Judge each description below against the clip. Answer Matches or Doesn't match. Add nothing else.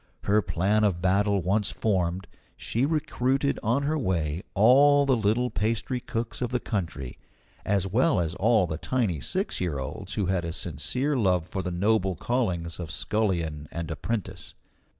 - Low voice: Matches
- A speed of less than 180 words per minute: Matches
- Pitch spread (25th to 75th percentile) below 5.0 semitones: Doesn't match